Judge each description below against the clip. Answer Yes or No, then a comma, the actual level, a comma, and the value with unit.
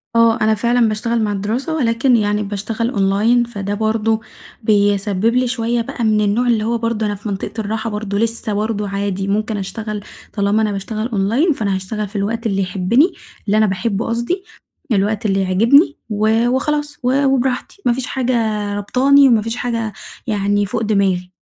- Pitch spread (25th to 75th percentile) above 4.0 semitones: No, narrow, 2.6 semitones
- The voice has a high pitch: Yes, high, 220 Hz